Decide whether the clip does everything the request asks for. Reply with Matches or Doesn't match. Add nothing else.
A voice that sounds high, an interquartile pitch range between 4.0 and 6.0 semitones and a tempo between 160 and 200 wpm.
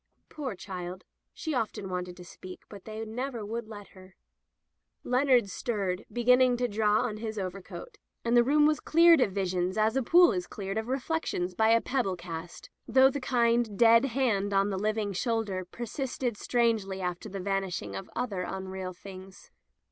Matches